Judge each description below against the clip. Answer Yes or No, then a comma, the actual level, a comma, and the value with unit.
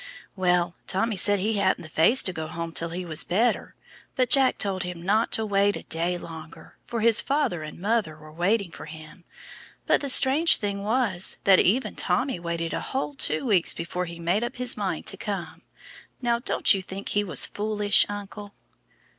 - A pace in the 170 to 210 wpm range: Yes, average, 195 wpm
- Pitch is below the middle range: No, high, 195 Hz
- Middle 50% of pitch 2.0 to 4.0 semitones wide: No, average, 4.8 semitones